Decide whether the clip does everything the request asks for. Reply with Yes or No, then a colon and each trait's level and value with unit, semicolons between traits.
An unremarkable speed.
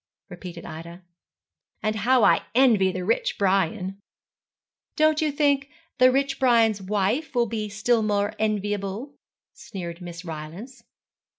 No: slow, 125 wpm